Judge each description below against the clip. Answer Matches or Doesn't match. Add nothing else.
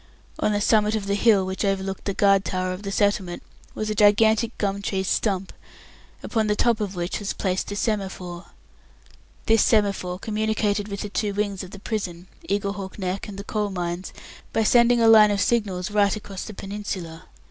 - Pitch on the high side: Matches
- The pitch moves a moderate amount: Doesn't match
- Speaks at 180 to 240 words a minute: Matches